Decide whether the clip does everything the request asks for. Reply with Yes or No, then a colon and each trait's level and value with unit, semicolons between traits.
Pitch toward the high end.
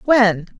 Yes: high, 215 Hz